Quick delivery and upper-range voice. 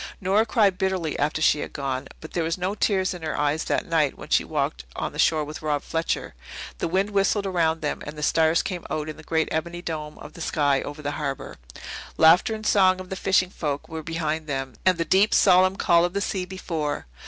No: fast, 230 wpm; medium, 165 Hz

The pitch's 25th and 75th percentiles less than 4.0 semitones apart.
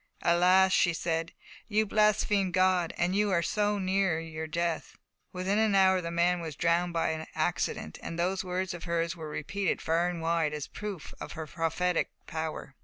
Yes: narrow, 2.4 semitones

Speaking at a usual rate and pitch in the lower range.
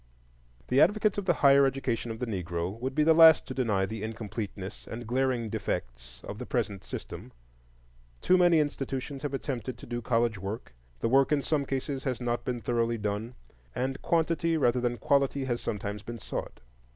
Yes: average, 185 wpm; low, 120 Hz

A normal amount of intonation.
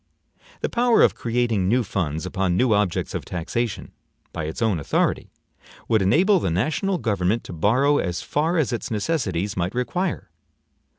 No: wide, 7.6 semitones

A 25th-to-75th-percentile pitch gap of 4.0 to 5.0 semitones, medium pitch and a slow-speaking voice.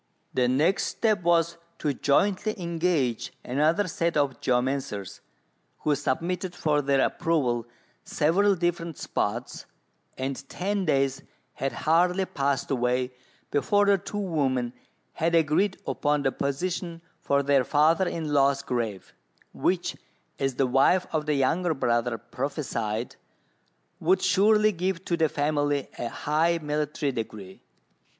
Yes: average, 4.5 semitones; medium, 150 Hz; slow, 130 wpm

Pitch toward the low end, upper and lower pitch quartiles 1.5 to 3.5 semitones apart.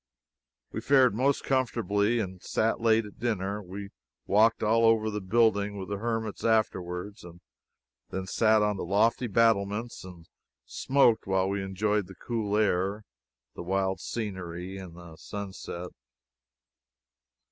Yes: low, 105 Hz; average, 3.0 semitones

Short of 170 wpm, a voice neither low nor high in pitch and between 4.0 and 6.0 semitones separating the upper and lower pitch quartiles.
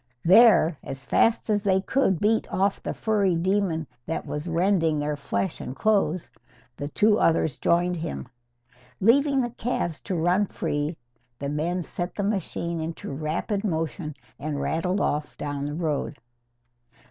Yes: average, 150 wpm; medium, 170 Hz; average, 4.6 semitones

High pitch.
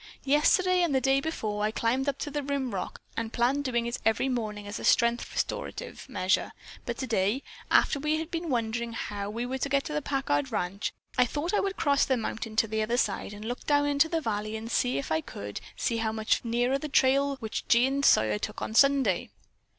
Yes: high, 245 Hz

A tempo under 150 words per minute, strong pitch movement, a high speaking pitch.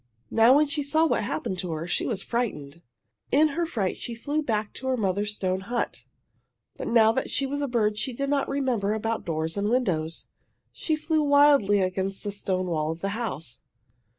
No: fast, 205 wpm; wide, 6.7 semitones; high, 220 Hz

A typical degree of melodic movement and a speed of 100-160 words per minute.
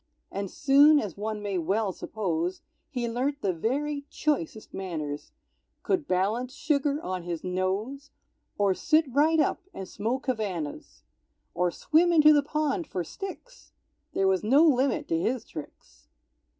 No: wide, 7.7 semitones; average, 145 wpm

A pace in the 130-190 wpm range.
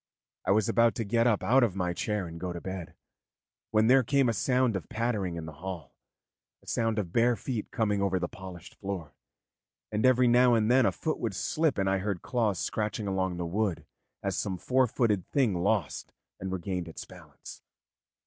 No: average, 200 wpm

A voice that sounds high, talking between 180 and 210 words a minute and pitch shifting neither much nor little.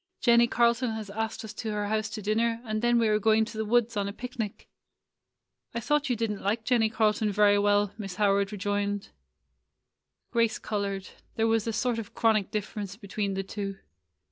No: high, 215 Hz; average, 195 wpm; narrow, 2.0 semitones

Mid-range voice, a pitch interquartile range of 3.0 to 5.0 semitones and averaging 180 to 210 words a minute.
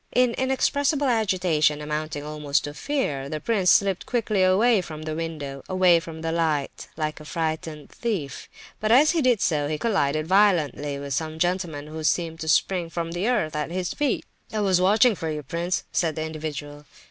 Yes: medium, 165 Hz; average, 4.6 semitones; average, 185 wpm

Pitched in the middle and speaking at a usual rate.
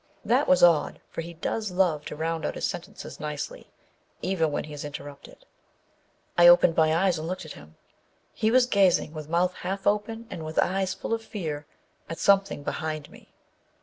Yes: medium, 170 Hz; average, 185 wpm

